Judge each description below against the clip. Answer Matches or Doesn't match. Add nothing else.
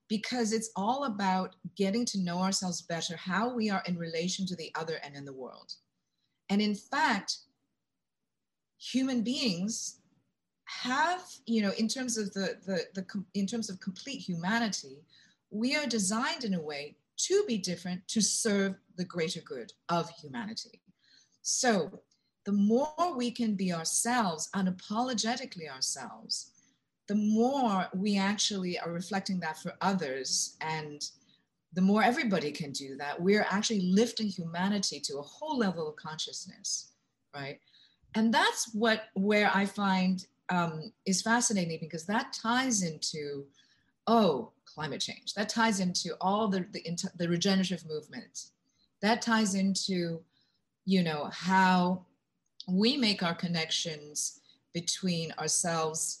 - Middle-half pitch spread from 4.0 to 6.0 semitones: Matches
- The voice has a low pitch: Doesn't match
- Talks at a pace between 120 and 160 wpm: Matches